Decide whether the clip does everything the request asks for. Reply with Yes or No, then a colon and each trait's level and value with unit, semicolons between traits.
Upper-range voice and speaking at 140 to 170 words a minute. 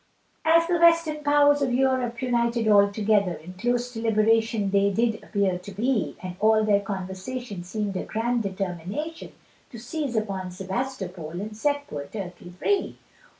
Yes: high, 220 Hz; average, 150 wpm